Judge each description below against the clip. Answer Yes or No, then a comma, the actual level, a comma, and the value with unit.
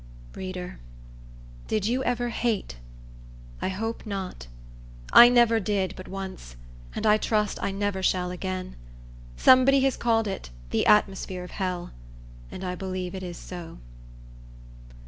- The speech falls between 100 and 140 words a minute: Yes, slow, 135 wpm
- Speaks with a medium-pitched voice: No, high, 195 Hz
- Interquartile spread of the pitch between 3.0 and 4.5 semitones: Yes, average, 3.4 semitones